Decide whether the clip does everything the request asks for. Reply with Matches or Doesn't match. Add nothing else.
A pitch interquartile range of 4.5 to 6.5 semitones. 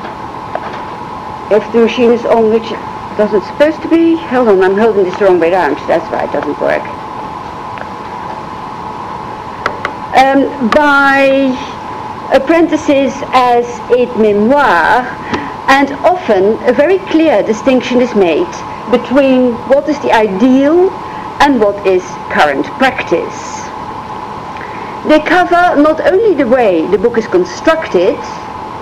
Matches